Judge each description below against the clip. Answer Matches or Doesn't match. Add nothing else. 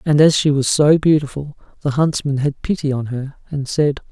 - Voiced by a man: Matches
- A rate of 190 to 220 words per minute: Matches